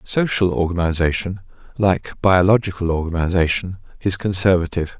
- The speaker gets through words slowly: Yes, slow, 85 wpm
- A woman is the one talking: No, male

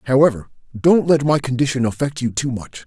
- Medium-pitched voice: No, low, 130 Hz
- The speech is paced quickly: No, average, 190 wpm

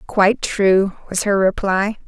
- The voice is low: No, high, 200 Hz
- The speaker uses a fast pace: No, average, 145 wpm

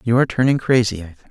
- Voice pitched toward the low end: Yes, low, 115 Hz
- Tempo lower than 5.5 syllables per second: No, 8.3 syllables/s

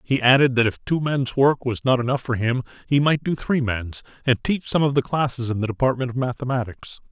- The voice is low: Yes, low, 130 Hz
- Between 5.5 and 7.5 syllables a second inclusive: Yes, 5.6 syllables/s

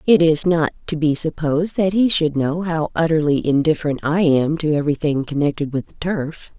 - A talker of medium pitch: Yes, medium, 155 Hz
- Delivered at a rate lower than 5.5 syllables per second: Yes, 5.3 syllables/s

